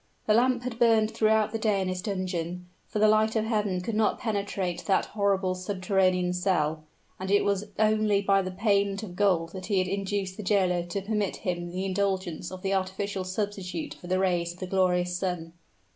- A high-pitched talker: Yes, high, 195 Hz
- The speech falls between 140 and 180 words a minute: No, average, 200 wpm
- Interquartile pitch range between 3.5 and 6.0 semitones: No, narrow, 2.4 semitones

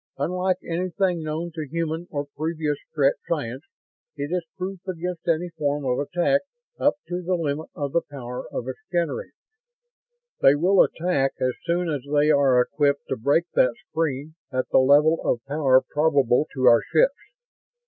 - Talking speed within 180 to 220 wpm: No, average, 165 wpm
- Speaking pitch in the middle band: Yes, medium, 155 Hz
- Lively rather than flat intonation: No, average, 3.7 semitones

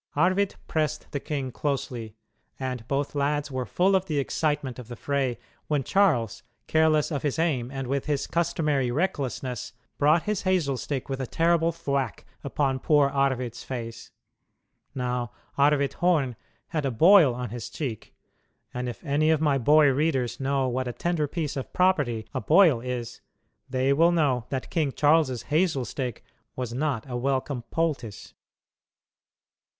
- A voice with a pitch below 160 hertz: Yes, medium, 140 Hz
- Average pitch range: Yes, average, 3.6 semitones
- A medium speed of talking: Yes, average, 155 wpm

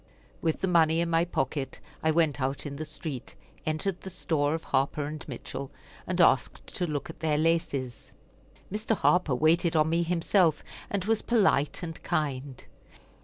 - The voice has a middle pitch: Yes, medium, 160 Hz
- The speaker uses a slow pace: No, average, 170 wpm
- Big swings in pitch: No, average, 3.1 semitones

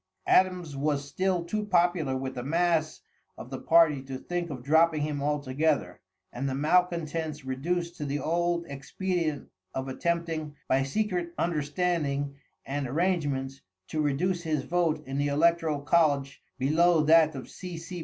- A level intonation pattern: No, average, 3.5 semitones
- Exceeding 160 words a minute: No, average, 150 wpm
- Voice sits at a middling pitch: Yes, medium, 155 Hz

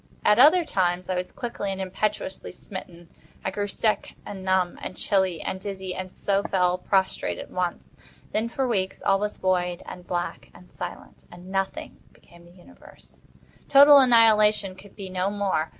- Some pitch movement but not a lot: No, narrow, 2.3 semitones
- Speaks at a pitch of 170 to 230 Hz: Yes, high, 190 Hz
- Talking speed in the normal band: Yes, average, 170 wpm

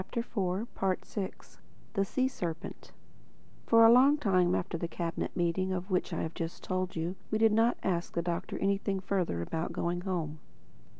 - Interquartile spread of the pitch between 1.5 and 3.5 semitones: Yes, average, 3.0 semitones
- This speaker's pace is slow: No, average, 175 wpm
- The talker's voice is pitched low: No, medium, 185 Hz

